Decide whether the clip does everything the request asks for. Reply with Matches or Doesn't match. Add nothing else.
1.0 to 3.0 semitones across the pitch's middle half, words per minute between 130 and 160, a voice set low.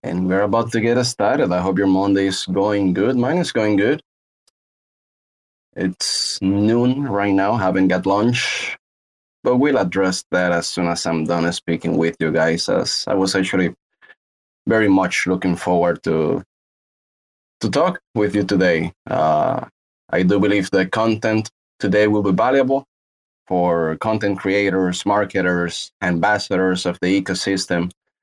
Matches